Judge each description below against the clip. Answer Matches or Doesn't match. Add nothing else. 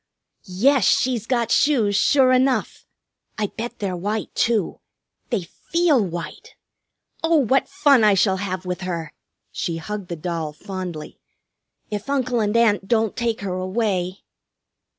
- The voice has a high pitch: Matches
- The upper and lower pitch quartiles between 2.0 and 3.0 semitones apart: Doesn't match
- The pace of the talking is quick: Doesn't match